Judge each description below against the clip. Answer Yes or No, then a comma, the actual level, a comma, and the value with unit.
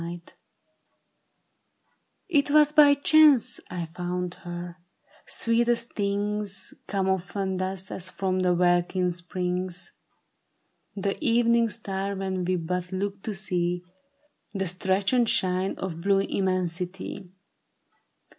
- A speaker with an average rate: No, slow, 110 wpm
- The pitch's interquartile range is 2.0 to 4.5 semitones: Yes, narrow, 2.4 semitones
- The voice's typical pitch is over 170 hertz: Yes, high, 190 Hz